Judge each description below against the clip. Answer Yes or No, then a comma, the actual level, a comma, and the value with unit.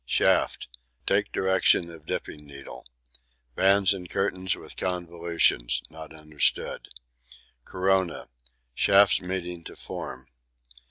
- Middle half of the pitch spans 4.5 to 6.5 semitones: No, average, 3.5 semitones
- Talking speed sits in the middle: No, slow, 100 wpm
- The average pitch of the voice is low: Yes, very low, 85 Hz